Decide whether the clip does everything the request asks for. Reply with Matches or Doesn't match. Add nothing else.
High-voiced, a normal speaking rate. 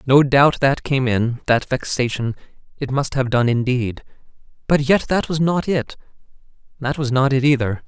Doesn't match